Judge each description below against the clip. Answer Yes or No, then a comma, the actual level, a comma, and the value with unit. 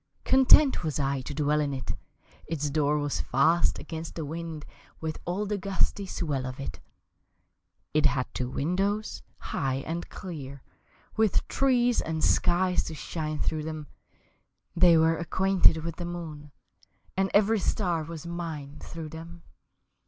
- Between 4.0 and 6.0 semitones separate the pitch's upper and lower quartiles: No, average, 3.3 semitones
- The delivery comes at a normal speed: Yes, average, 145 wpm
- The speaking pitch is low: No, medium, 160 Hz